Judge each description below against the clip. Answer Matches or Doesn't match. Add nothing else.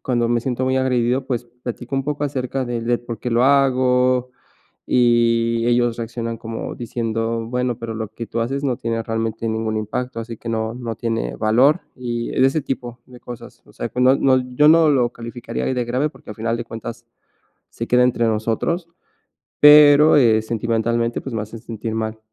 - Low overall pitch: Matches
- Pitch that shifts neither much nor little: Doesn't match